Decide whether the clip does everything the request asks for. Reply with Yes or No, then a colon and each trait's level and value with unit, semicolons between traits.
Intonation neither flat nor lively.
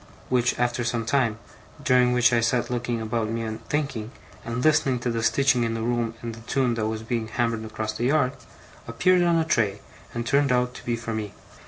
No: narrow, 1.8 semitones